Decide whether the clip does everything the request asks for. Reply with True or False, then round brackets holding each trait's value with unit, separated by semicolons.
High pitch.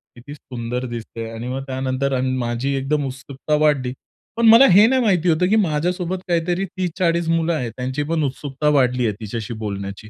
False (140 Hz)